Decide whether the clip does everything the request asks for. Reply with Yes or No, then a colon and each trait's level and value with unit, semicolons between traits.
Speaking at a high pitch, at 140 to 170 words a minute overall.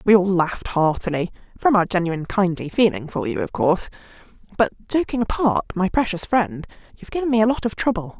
No: high, 200 Hz; average, 185 wpm